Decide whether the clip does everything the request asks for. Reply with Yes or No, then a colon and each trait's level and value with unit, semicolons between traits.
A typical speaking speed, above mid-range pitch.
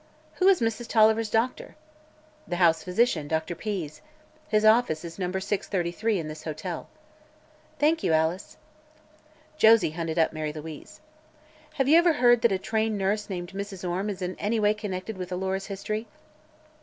Yes: average, 160 wpm; high, 195 Hz